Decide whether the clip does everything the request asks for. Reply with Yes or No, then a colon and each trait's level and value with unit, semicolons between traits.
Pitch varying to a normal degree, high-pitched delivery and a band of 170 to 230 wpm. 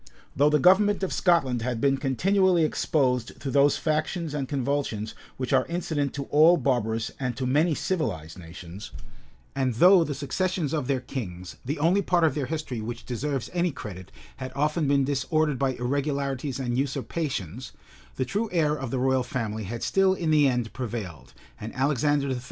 No: average, 3.9 semitones; medium, 140 Hz; average, 175 wpm